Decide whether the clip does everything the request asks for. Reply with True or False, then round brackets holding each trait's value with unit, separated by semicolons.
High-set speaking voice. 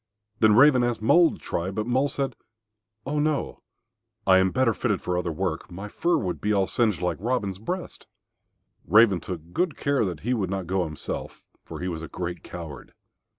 False (100 Hz)